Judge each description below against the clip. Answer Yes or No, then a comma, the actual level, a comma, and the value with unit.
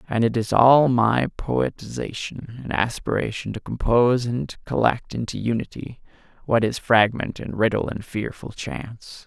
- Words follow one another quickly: No, average, 140 wpm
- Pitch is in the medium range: No, low, 115 Hz